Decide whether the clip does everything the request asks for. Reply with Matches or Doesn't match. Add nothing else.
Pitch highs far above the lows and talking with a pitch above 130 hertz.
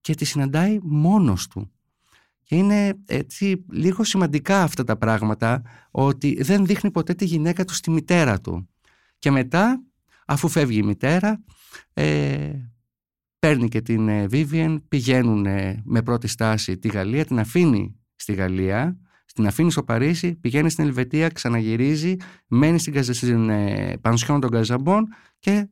Matches